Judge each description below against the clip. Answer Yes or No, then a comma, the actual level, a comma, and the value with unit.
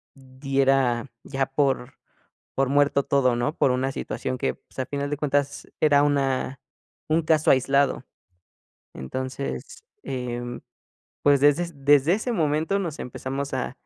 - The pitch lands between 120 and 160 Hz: Yes, medium, 140 Hz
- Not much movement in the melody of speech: Yes, narrow, 1.9 semitones